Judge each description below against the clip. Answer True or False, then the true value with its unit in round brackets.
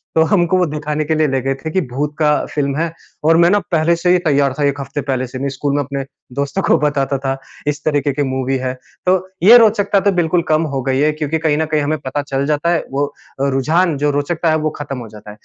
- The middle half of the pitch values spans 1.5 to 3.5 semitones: True (2.9 semitones)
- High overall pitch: False (150 Hz)